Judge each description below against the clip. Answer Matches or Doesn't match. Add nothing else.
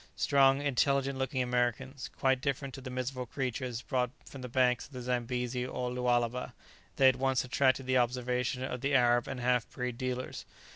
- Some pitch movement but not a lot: Doesn't match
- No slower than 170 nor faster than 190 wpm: Matches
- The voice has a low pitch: Matches